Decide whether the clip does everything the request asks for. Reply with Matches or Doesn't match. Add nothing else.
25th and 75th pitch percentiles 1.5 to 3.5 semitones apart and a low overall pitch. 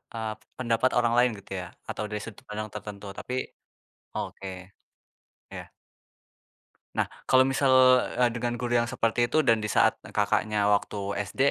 Matches